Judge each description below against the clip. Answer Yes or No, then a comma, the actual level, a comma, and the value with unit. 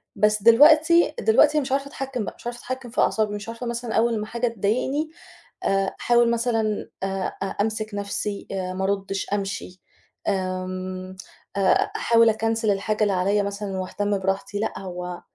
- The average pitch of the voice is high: Yes, high, 210 Hz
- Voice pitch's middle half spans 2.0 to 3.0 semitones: No, average, 3.4 semitones